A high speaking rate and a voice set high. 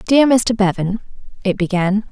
No: average, 140 wpm; high, 210 Hz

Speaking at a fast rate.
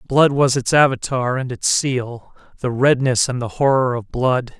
No: average, 170 wpm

